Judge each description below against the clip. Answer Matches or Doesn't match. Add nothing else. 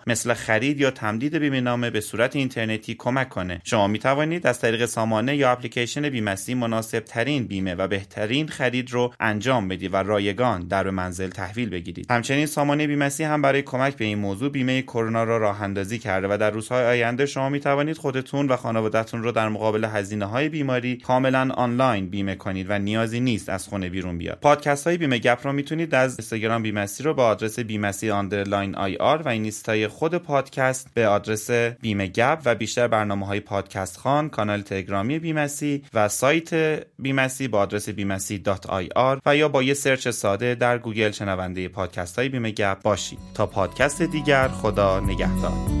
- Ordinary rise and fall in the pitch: Matches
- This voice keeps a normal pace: Doesn't match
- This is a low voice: Matches